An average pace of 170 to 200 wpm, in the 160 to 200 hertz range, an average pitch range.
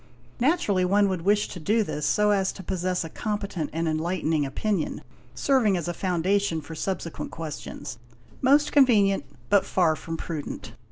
No: average, 160 wpm; medium, 185 Hz; average, 4.0 semitones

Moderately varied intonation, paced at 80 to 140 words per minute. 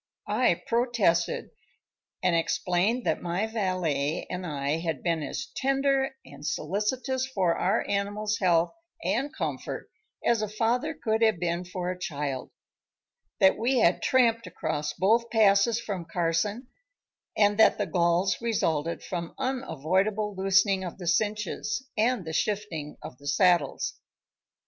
Yes: average, 4.7 semitones; slow, 135 wpm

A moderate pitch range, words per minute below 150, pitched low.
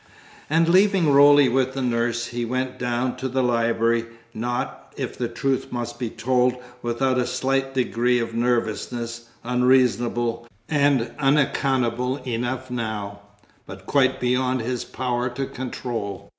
No: narrow, 1.9 semitones; slow, 135 wpm; low, 125 Hz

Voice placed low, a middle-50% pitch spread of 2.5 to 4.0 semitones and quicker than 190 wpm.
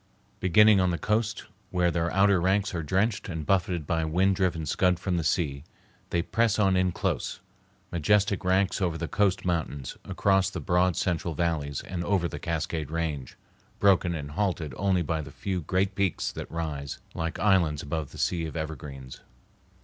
No: very low, 85 Hz; average, 3.3 semitones; average, 175 wpm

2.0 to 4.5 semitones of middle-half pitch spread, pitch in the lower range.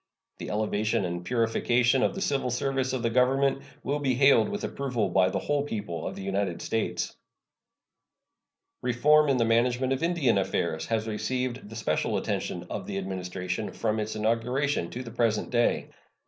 Yes: average, 4.2 semitones; low, 115 Hz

